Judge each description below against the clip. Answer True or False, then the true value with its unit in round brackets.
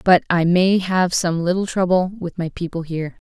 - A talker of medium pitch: True (175 Hz)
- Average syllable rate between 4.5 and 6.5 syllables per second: True (5.0 syllables/s)